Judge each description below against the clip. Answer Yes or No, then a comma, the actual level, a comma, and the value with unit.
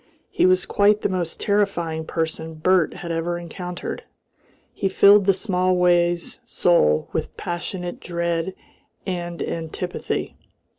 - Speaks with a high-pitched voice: No, medium, 175 Hz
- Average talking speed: No, slow, 115 wpm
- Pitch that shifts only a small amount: Yes, narrow, 1.7 semitones